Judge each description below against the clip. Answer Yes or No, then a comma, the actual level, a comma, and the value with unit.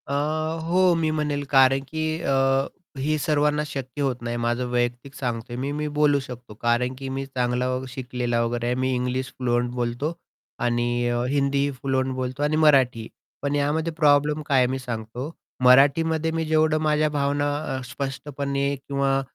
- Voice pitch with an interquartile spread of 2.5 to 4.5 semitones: Yes, average, 3.0 semitones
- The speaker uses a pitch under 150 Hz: Yes, low, 135 Hz